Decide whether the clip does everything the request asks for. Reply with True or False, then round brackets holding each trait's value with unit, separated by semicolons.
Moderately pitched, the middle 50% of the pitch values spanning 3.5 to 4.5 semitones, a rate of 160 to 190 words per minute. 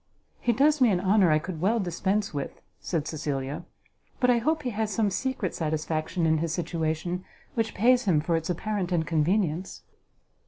False (180 Hz; 5.2 semitones; 170 wpm)